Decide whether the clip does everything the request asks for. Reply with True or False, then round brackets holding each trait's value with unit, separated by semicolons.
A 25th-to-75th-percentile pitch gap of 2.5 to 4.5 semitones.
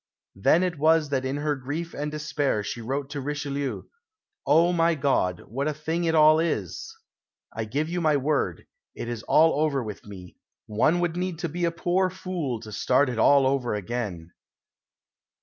False (4.9 semitones)